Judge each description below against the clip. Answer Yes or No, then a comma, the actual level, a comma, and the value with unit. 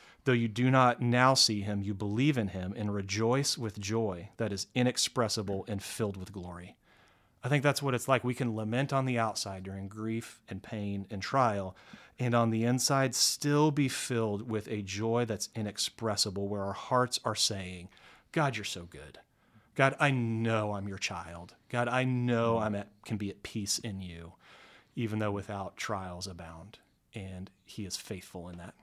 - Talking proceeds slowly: No, average, 185 wpm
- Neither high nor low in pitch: No, low, 110 Hz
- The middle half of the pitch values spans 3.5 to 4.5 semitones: Yes, average, 3.8 semitones